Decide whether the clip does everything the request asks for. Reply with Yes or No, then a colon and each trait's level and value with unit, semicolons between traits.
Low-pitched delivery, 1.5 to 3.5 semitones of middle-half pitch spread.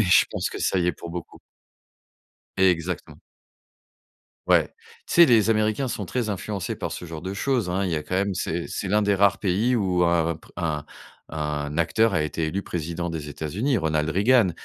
No: very low, 90 Hz; average, 4.1 semitones